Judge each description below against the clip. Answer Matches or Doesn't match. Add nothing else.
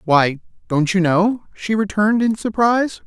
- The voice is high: Matches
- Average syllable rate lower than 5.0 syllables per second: Matches